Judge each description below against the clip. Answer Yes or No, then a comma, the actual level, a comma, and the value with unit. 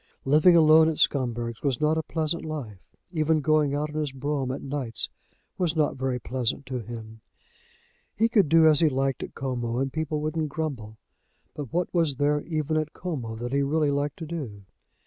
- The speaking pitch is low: No, medium, 145 Hz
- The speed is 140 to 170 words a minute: No, average, 190 wpm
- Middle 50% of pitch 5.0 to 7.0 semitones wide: No, average, 3.3 semitones